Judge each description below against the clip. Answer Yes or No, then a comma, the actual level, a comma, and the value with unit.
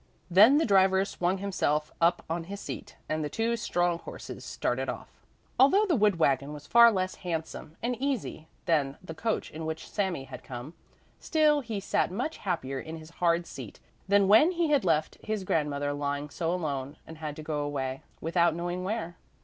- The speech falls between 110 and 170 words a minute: No, average, 190 wpm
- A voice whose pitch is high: No, medium, 170 Hz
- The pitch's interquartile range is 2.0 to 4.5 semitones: No, average, 5.3 semitones